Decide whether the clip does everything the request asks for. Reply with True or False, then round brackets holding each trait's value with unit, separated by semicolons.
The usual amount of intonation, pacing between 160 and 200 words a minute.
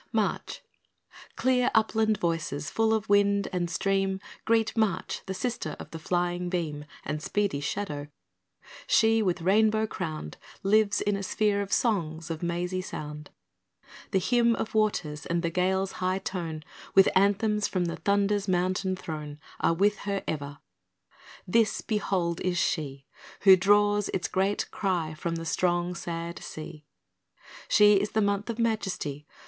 False (3.7 semitones; 150 wpm)